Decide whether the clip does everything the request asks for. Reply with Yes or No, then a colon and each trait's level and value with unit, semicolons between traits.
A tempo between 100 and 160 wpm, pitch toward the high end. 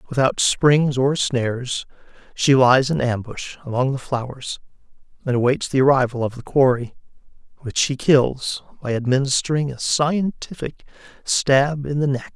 No: average, 140 wpm; low, 135 Hz